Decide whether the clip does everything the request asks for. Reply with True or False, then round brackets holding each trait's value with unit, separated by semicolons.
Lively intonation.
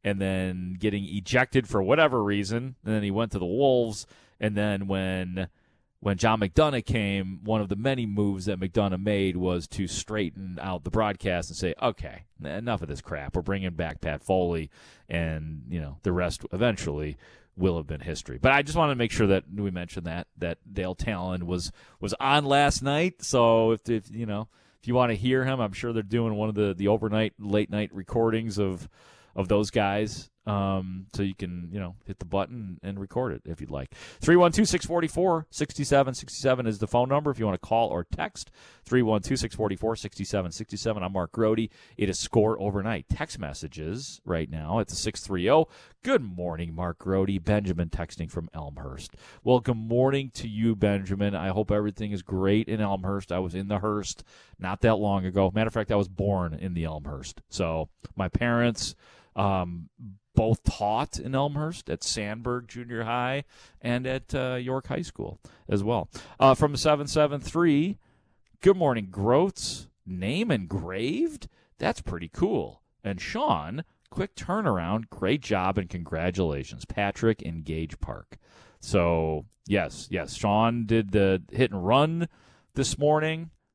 False (4.2 semitones)